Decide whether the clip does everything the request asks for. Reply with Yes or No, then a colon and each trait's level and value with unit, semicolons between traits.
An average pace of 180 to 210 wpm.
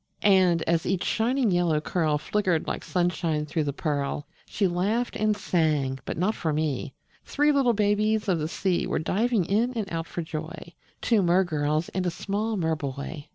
Yes: average, 185 wpm